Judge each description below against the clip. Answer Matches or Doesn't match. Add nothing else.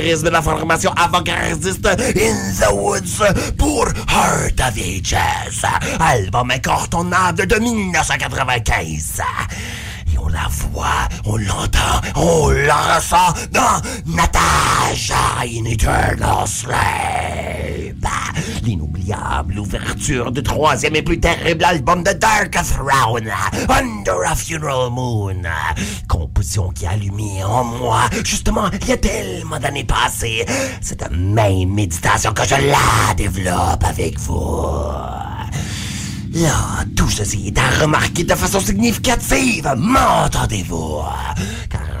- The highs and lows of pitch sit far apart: Matches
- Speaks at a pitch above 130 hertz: Doesn't match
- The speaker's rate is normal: Doesn't match